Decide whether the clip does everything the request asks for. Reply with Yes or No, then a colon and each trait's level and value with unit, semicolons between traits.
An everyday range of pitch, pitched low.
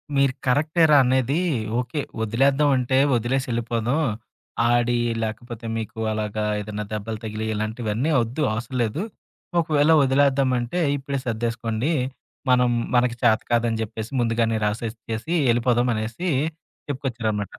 Yes: average, 3.1 semitones; low, 120 Hz